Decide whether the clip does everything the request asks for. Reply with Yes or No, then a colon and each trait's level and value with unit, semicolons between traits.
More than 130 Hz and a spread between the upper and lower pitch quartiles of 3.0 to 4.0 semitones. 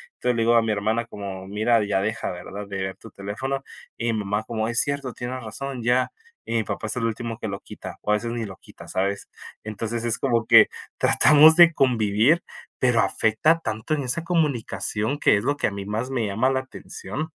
No: low, 115 Hz; average, 3.5 semitones